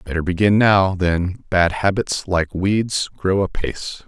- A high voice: No, very low, 95 Hz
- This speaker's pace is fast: No, average, 145 wpm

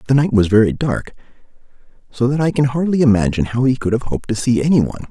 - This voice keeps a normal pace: No, fast, 225 wpm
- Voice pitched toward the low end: Yes, low, 120 Hz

